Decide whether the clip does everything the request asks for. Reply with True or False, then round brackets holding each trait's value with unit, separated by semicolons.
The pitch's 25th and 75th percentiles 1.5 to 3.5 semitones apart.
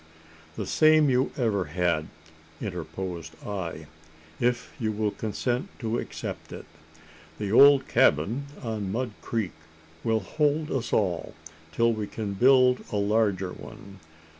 False (4.7 semitones)